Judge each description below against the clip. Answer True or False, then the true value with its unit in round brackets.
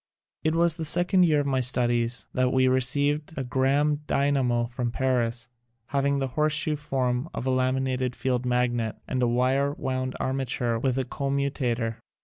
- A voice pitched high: False (130 Hz)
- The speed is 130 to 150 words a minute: False (180 wpm)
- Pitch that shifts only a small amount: True (2.2 semitones)